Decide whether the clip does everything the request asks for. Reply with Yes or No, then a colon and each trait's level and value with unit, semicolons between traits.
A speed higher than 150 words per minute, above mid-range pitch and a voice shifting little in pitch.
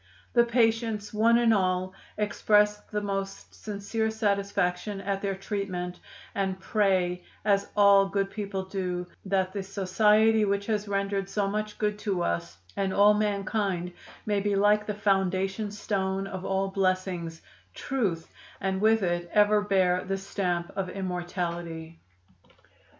No: average, 140 wpm; high, 195 Hz; narrow, 2.0 semitones